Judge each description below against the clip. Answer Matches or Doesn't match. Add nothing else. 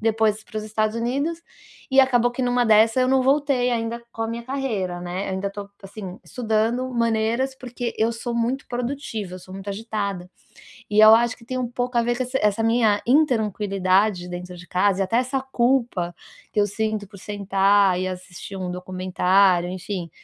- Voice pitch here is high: Matches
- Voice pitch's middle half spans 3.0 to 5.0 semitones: Matches